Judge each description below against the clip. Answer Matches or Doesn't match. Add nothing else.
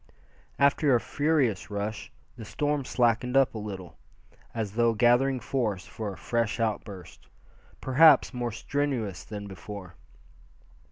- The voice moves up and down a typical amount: Matches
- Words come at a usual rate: Doesn't match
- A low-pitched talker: Matches